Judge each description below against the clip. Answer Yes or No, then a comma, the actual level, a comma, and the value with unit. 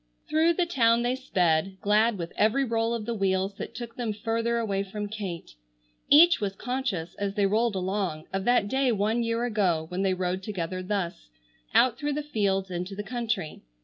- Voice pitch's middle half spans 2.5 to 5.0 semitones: Yes, average, 3.7 semitones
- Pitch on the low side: No, high, 210 Hz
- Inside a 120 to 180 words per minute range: No, average, 190 wpm